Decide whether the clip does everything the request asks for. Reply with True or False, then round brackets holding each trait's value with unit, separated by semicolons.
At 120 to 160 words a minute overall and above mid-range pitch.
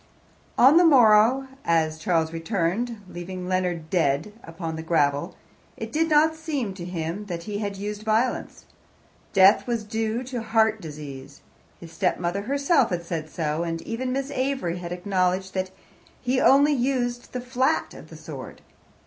True (155 wpm; 200 Hz)